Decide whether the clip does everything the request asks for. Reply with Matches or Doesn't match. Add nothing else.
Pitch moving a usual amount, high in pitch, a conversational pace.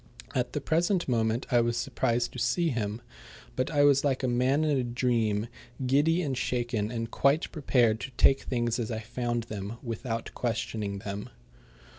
Doesn't match